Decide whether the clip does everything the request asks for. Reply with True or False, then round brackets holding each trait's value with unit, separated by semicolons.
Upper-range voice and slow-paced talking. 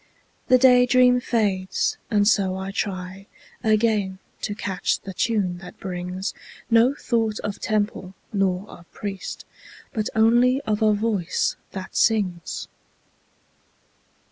True (205 Hz; 120 wpm)